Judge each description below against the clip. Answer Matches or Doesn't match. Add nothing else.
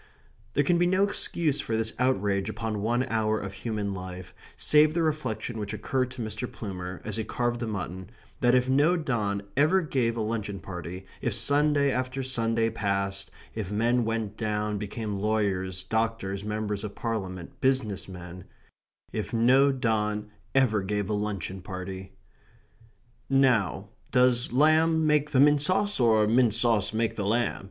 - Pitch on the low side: Matches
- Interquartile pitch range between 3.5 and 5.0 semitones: Matches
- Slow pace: Doesn't match